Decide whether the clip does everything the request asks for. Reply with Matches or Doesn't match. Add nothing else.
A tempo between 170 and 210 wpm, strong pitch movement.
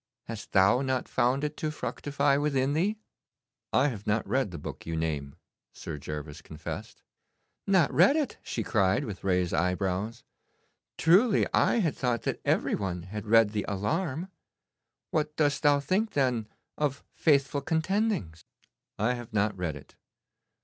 Doesn't match